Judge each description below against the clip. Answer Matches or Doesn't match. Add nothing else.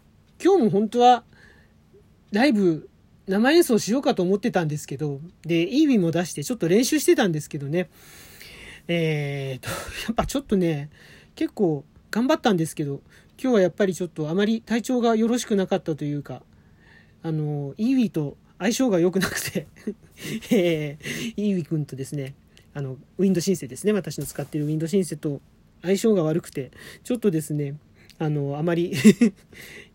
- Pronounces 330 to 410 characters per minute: Matches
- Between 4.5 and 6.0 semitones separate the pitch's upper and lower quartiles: Doesn't match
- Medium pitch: Matches